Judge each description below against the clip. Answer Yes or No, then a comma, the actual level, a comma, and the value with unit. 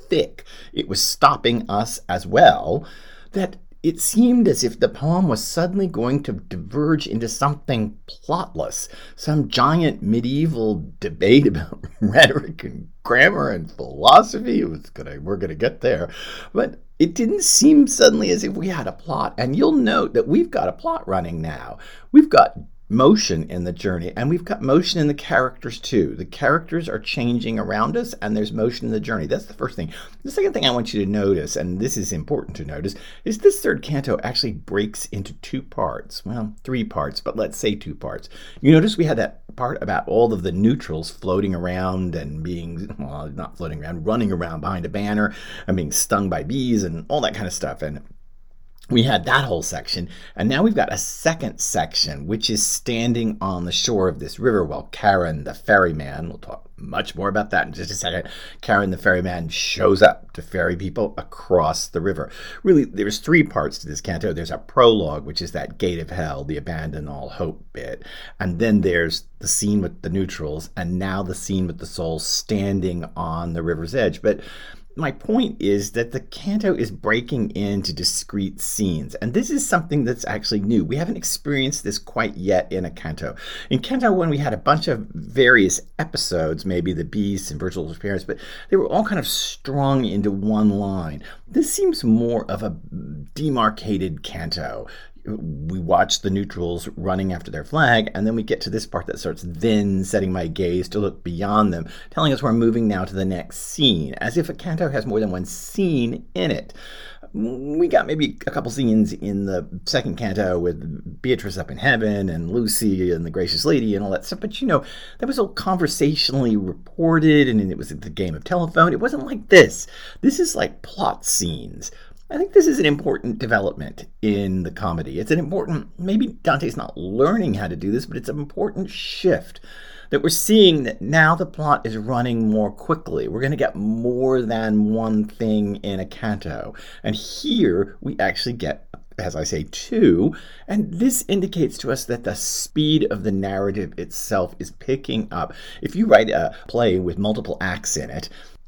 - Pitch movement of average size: No, wide, 8.6 semitones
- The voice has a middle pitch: No, low, 110 Hz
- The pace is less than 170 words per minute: No, average, 195 wpm